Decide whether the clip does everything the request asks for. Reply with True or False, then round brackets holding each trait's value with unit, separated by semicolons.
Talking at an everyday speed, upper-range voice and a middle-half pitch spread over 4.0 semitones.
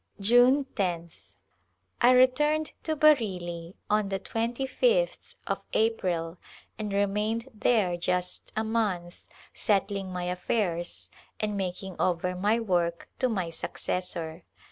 False (120 wpm; 200 Hz; 4.5 semitones)